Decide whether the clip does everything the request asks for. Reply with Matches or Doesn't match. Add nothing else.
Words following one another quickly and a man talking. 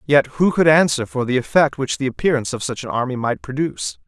Matches